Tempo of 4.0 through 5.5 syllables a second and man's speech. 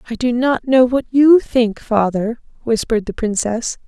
No: 4.5 syllables/s; female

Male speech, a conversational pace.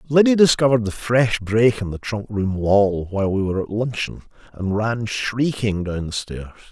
Yes: male; average, 190 wpm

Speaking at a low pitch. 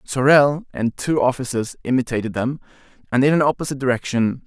Yes: low, 130 Hz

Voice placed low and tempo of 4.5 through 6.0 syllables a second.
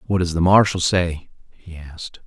Yes: very low, 85 Hz; 5.1 syllables/s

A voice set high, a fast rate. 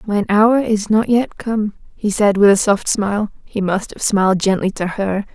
Yes: high, 205 Hz; fast, 215 wpm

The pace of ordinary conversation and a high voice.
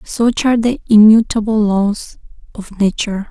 No: slow, 125 wpm; high, 215 Hz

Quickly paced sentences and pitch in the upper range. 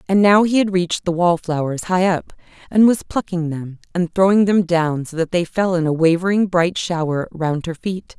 No: fast, 215 wpm; medium, 175 Hz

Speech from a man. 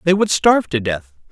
Yes: male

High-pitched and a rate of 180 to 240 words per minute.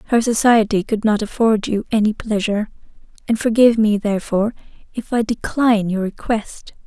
No: high, 215 Hz; average, 150 wpm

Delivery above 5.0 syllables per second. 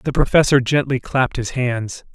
No: 4.9 syllables/s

